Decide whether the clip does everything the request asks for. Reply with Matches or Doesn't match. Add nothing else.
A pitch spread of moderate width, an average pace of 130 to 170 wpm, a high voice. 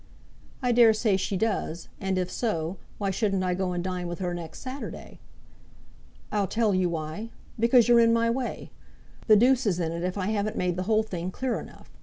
Doesn't match